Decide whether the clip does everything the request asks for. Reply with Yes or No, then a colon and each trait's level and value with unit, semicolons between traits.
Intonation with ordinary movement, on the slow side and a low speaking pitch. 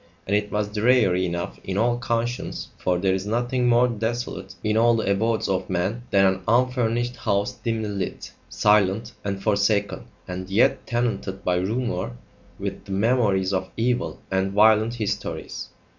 No: average, 3.5 semitones; average, 160 wpm; low, 105 Hz